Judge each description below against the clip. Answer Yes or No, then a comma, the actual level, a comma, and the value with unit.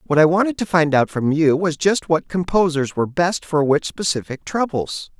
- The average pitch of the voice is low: No, medium, 165 Hz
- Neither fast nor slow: No, fast, 210 wpm